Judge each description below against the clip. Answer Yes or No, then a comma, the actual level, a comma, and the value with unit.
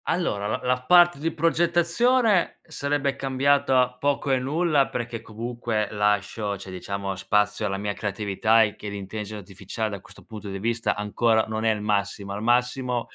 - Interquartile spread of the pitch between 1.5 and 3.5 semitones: No, average, 4.8 semitones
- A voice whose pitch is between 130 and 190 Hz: No, low, 115 Hz